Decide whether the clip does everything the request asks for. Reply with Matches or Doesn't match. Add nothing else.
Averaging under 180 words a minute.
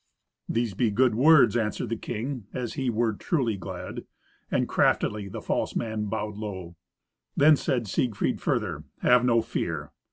Matches